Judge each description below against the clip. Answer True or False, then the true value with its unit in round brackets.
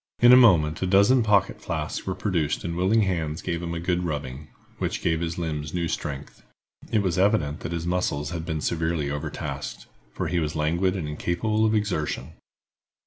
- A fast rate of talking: False (190 wpm)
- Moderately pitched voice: False (85 Hz)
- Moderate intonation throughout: True (3.6 semitones)